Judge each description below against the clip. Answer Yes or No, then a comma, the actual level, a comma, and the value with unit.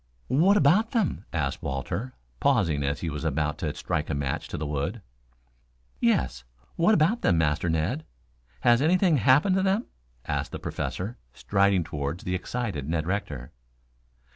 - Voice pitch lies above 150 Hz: No, very low, 90 Hz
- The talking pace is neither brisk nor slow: Yes, average, 155 wpm